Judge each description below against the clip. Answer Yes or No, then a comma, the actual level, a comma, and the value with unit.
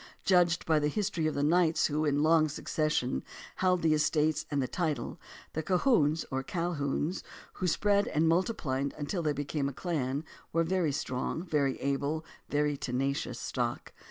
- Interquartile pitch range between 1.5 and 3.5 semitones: Yes, average, 3.0 semitones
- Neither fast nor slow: Yes, average, 165 wpm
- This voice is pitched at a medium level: Yes, medium, 155 Hz